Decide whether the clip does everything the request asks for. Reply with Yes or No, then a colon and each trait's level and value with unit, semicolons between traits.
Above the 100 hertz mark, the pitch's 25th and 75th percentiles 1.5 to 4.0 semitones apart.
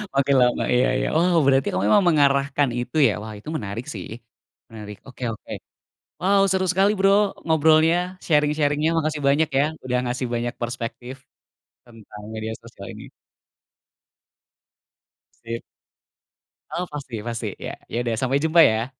No: low, 135 Hz; average, 5.0 semitones